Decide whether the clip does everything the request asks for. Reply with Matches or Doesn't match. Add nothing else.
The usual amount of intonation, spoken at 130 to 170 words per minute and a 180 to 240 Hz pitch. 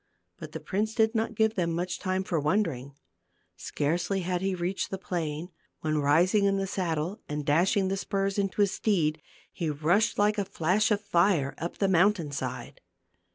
Doesn't match